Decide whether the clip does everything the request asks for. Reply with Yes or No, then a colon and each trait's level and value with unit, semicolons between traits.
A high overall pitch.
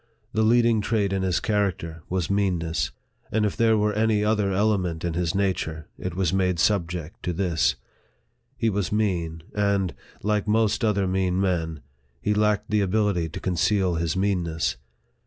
No: very low, 95 Hz